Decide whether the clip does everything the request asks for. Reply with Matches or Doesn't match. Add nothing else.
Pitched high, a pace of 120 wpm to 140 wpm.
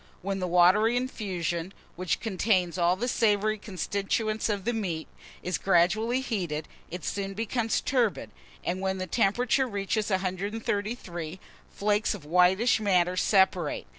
Matches